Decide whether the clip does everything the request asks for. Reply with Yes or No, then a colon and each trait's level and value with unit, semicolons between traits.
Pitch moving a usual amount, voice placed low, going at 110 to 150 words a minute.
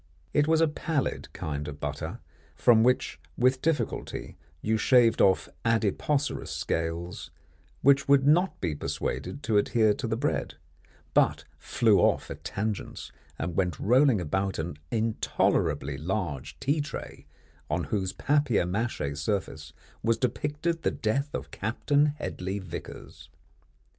No: wide, 7.8 semitones; low, 110 Hz; slow, 135 wpm